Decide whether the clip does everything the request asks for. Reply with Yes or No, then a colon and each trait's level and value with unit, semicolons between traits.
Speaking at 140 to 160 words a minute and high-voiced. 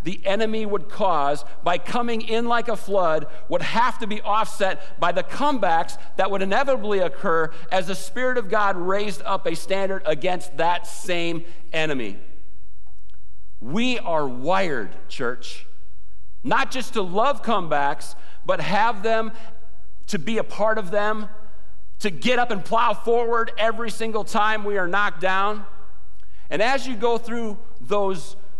Yes: average, 150 wpm; high, 200 Hz